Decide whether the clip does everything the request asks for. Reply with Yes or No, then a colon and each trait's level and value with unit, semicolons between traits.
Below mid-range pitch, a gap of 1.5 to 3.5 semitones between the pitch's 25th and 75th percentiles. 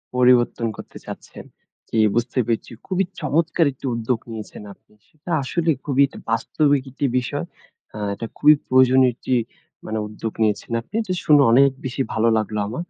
No: low, 130 Hz; average, 4.2 semitones